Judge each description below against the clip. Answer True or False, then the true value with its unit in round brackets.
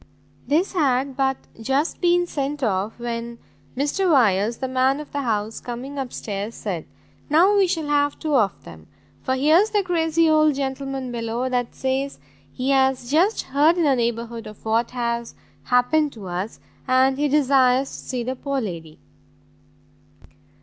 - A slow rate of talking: False (165 wpm)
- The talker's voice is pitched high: True (265 Hz)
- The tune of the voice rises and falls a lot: False (3.8 semitones)